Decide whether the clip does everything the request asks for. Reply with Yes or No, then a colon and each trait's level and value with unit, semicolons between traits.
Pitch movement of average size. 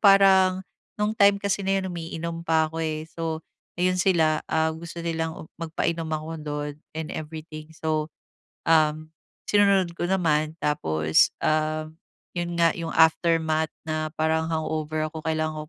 No: narrow, 1.7 semitones